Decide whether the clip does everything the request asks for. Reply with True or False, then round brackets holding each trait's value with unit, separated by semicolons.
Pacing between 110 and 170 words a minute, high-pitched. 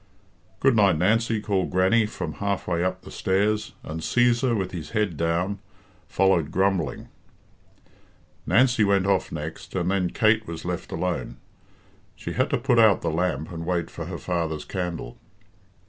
False (160 wpm; 95 Hz)